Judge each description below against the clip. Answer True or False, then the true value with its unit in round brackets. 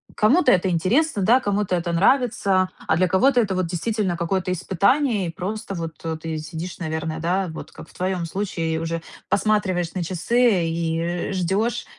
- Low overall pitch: False (185 Hz)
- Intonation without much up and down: False (3.8 semitones)